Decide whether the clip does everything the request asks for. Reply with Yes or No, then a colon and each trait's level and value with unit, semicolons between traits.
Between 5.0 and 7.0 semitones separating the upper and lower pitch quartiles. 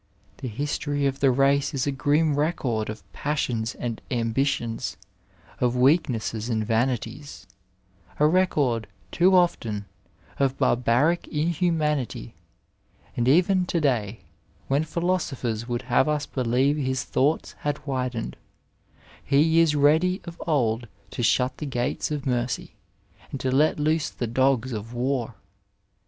No: average, 4.0 semitones